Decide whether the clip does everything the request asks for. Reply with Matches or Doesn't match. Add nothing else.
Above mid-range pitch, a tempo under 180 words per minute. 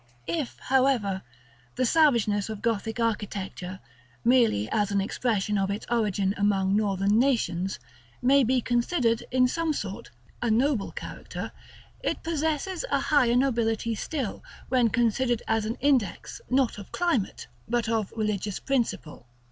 Matches